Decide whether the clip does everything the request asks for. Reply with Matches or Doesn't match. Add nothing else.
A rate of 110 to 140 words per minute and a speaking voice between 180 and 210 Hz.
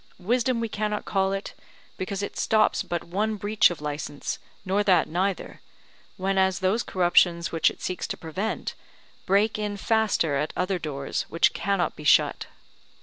Doesn't match